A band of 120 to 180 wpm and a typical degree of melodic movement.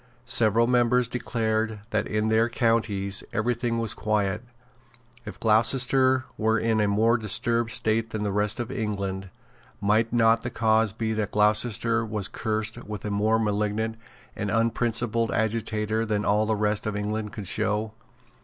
No: average, 155 wpm; narrow, 1.5 semitones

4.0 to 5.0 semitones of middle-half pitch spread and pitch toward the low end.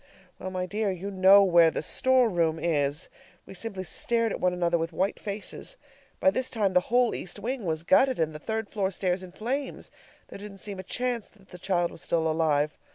No: average, 4.4 semitones; high, 190 Hz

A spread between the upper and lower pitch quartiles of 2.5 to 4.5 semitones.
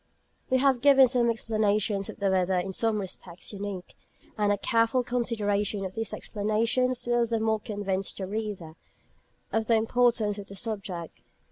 Yes: average, 2.8 semitones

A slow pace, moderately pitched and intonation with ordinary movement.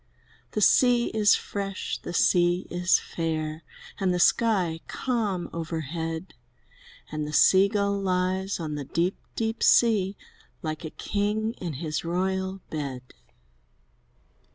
Yes: slow, 125 wpm; medium, 180 Hz; average, 3.7 semitones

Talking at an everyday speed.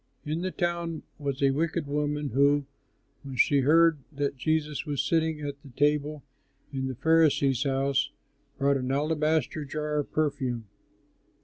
Yes: average, 145 wpm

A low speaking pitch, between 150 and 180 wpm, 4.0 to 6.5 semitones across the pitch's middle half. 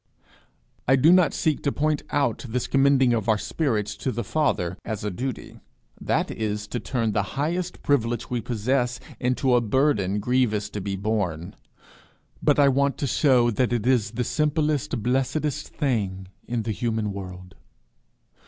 Yes: low, 120 Hz; average, 160 wpm; average, 4.7 semitones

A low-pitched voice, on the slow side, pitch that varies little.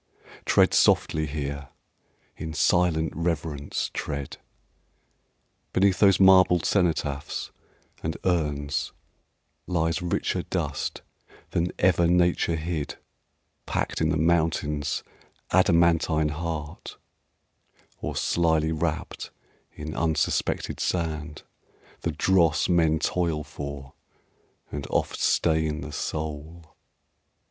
Yes: very low, 80 Hz; slow, 90 wpm; narrow, 2.2 semitones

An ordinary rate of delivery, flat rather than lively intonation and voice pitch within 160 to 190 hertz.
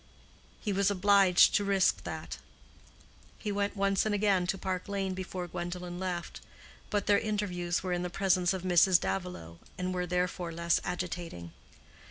Yes: average, 160 wpm; narrow, 2.0 semitones; medium, 185 Hz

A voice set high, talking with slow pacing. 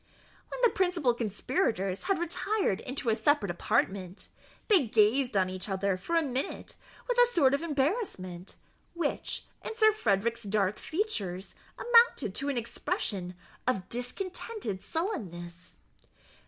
Yes: high, 245 Hz; slow, 130 wpm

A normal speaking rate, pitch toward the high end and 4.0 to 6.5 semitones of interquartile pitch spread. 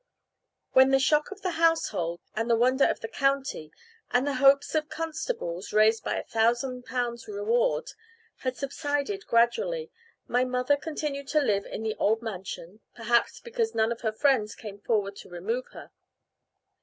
Yes: average, 165 wpm; very high, 255 Hz; average, 5.3 semitones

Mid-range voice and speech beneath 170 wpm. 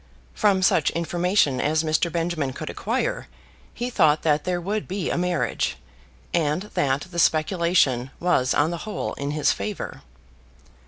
Yes: medium, 170 Hz; average, 150 wpm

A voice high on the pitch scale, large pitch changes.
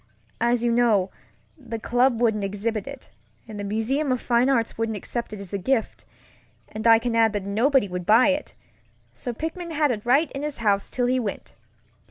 No: high, 235 Hz; average, 3.5 semitones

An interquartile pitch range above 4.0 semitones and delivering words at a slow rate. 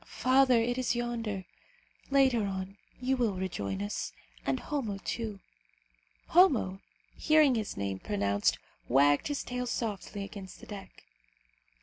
Yes: average, 5.0 semitones; slow, 125 wpm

